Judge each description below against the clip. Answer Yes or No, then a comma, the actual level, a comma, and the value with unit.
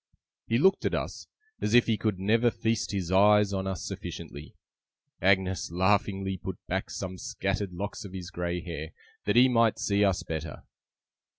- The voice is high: No, very low, 95 Hz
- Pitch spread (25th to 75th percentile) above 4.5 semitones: No, narrow, 2.6 semitones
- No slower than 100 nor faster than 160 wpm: No, average, 170 wpm